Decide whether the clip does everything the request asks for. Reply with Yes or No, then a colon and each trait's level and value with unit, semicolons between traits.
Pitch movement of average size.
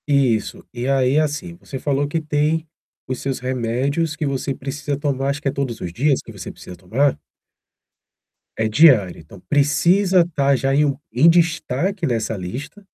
Yes: average, 3.4 semitones